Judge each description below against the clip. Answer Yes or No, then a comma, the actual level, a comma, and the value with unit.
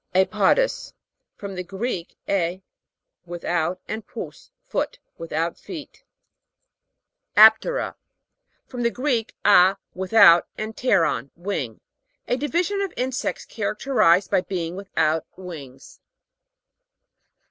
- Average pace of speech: No, slow, 105 wpm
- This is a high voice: Yes, high, 195 Hz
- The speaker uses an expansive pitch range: Yes, wide, 5.9 semitones